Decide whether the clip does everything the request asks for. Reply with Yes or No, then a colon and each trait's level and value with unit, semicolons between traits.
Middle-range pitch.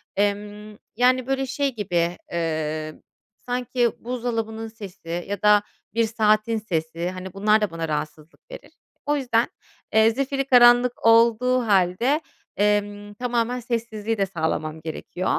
No: high, 215 Hz